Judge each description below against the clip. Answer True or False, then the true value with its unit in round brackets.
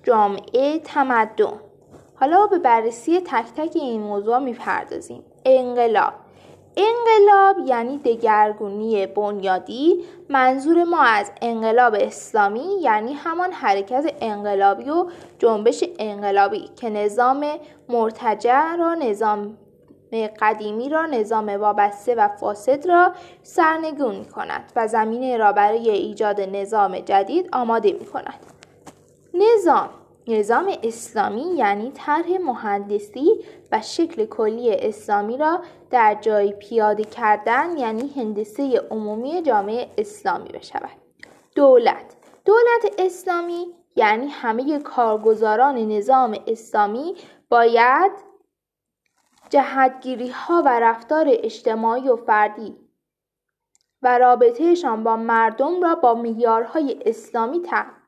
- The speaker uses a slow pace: True (100 wpm)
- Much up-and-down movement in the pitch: True (8.0 semitones)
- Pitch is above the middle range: True (250 Hz)